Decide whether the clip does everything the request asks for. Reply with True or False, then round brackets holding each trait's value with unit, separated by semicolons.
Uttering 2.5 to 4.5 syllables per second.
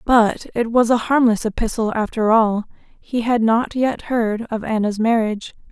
True (4.4 syllables/s)